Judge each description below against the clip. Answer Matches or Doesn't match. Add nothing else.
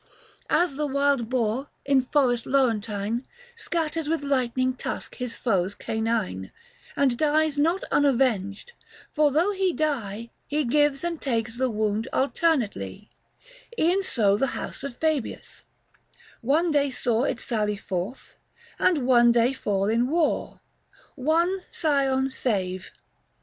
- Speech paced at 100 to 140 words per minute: Matches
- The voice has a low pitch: Doesn't match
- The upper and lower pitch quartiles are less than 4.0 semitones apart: Doesn't match